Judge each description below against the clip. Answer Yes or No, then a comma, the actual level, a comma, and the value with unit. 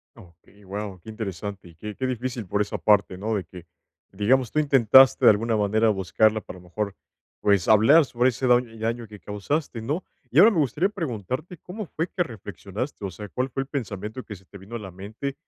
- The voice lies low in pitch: Yes, low, 110 Hz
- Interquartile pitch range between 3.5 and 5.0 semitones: Yes, average, 4.5 semitones